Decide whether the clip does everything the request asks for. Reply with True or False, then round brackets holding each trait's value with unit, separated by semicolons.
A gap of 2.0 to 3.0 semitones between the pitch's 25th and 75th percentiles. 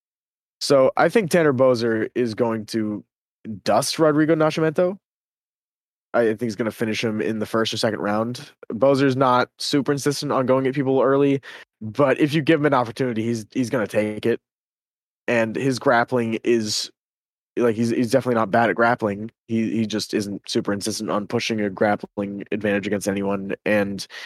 False (3.8 semitones)